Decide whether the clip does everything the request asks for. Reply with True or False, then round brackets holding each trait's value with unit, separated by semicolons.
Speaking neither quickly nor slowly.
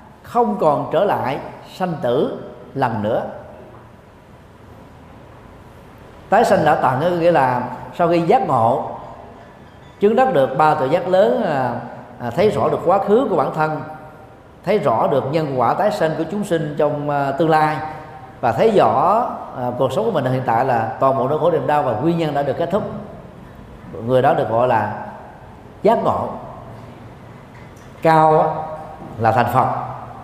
False (160 wpm)